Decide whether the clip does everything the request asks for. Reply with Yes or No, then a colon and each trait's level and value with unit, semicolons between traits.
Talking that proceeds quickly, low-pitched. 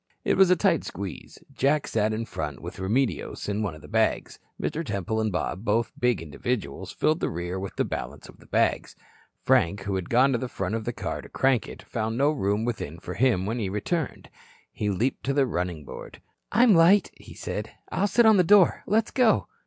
Yes: fast, 215 wpm; low, 115 Hz